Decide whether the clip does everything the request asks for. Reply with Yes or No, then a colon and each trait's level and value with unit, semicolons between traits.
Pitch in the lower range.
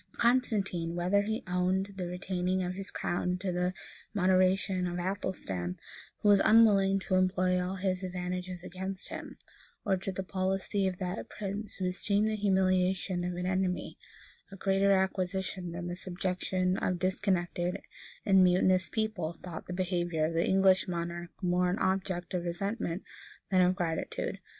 No: medium, 185 Hz